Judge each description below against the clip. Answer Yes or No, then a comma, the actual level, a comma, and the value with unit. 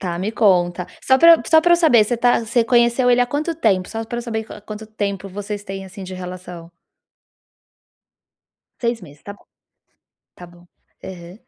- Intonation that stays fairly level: No, average, 4.6 semitones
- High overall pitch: Yes, high, 210 Hz